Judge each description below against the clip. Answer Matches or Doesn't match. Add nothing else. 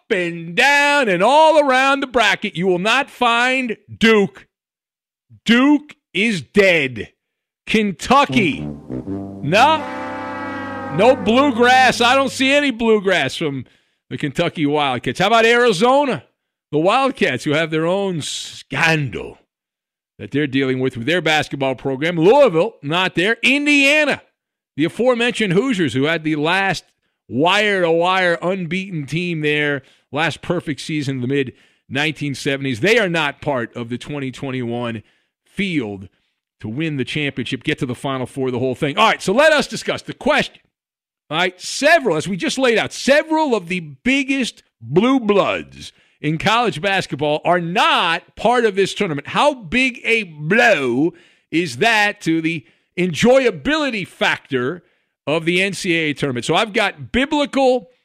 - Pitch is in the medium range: Matches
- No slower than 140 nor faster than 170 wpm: Matches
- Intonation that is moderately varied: Doesn't match